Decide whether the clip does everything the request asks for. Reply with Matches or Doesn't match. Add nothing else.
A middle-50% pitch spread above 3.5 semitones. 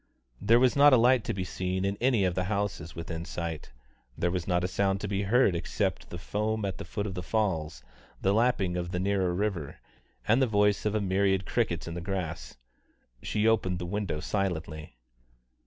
Doesn't match